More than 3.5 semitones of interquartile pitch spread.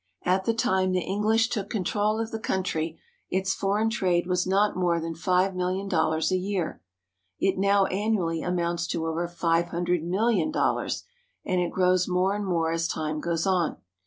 No: narrow, 2.5 semitones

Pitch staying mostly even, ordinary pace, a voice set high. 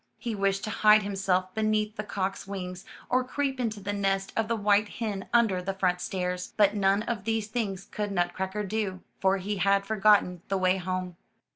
Yes: narrow, 2.1 semitones; average, 190 wpm; high, 200 Hz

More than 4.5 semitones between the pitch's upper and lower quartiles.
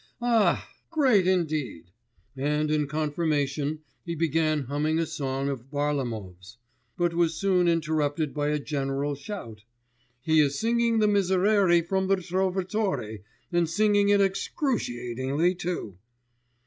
Yes: average, 5.1 semitones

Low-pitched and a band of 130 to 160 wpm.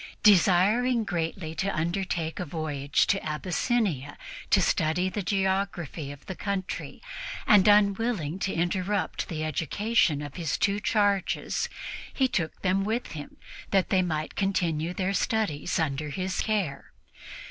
No: medium, 185 Hz; slow, 135 wpm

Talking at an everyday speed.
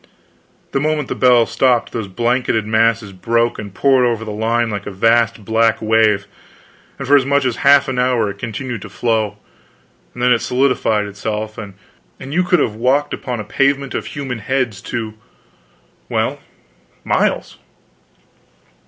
Yes: average, 160 wpm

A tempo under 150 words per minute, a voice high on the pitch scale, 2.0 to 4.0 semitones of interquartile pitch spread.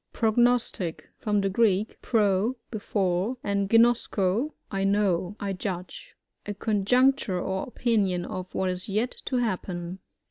Yes: slow, 135 wpm; high, 200 Hz; average, 3.5 semitones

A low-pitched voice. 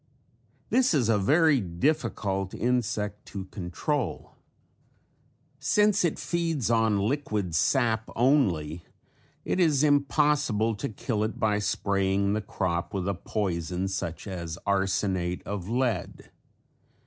Yes: low, 105 Hz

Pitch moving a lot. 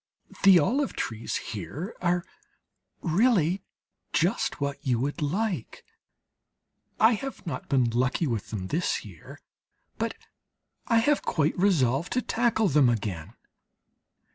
Yes: wide, 8.5 semitones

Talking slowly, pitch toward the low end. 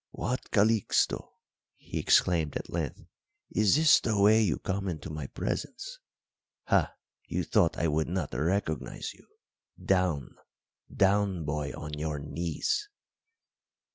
Yes: slow, 125 wpm; very low, 90 Hz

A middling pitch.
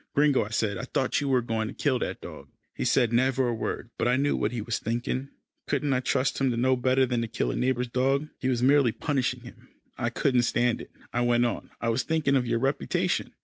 No: low, 125 Hz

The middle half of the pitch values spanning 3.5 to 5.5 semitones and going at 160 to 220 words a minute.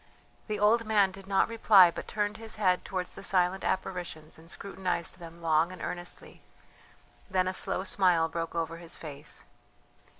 No: average, 2.8 semitones; average, 165 wpm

